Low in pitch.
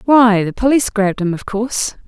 No: high, 220 Hz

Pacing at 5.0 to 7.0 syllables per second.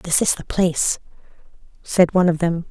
Yes: 5.5 syllables/s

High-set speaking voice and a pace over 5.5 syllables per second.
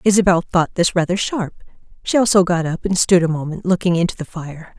No: medium, 180 Hz; 5.9 syllables/s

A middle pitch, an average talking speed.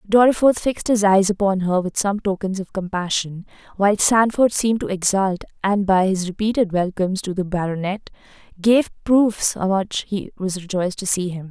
No: high, 195 Hz; average, 175 wpm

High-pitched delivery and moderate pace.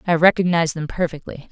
No: medium, 165 Hz; average, 160 wpm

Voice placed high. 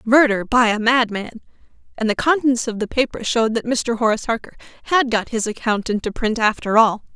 Yes: high, 230 Hz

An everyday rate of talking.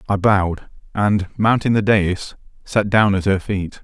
Yes: average, 170 wpm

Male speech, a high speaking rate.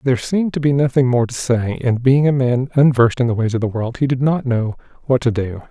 Yes: male; fast, 275 wpm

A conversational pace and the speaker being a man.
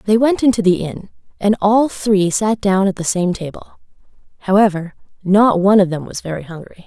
No: average, 190 wpm; female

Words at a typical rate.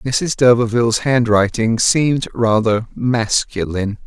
No: slow, 90 wpm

